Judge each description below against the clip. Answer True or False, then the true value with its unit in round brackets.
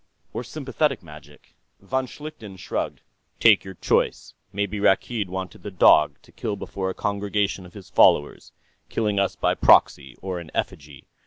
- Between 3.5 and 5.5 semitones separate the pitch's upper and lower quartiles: False (2.9 semitones)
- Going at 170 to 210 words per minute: False (155 wpm)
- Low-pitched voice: True (100 Hz)